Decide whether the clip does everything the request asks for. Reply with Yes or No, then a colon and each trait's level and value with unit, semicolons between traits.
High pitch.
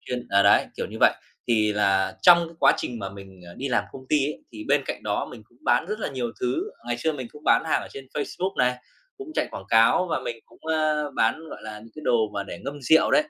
No: low, 125 Hz